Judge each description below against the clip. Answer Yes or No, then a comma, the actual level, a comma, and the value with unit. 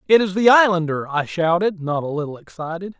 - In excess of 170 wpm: Yes, average, 200 wpm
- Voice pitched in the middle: Yes, medium, 175 Hz